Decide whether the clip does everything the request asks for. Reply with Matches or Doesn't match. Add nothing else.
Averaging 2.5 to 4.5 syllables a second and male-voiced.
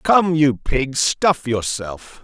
Matches